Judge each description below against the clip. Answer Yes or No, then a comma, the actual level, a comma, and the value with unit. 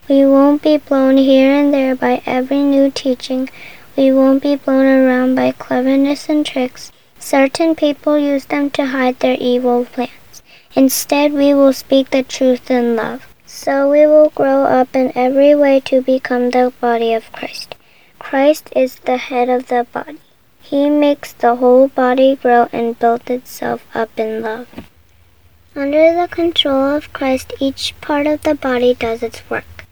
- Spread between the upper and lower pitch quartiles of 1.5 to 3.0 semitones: Yes, narrow, 2.4 semitones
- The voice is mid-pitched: No, very high, 265 Hz